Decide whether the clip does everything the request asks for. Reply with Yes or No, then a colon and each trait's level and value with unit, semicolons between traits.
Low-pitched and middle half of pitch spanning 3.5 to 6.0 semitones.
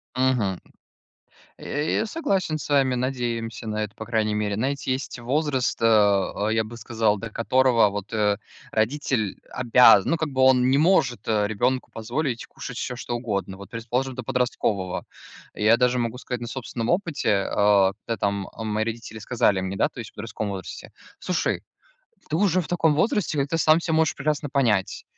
Yes: low, 120 Hz; average, 4.2 semitones